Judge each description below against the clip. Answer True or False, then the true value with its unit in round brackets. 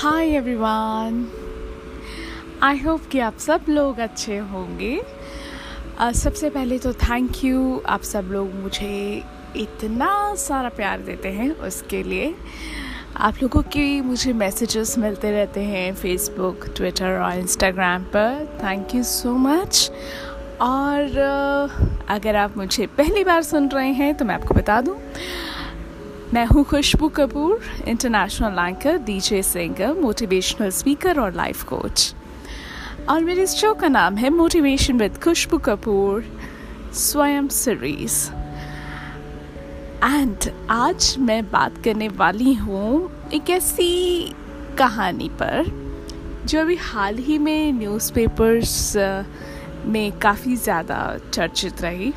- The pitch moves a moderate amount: False (6.2 semitones)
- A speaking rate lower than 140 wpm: True (120 wpm)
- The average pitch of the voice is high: True (235 Hz)